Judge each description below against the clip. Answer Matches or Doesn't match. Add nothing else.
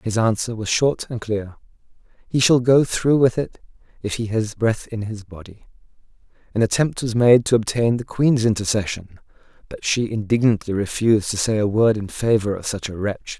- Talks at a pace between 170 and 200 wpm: Matches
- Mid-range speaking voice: Doesn't match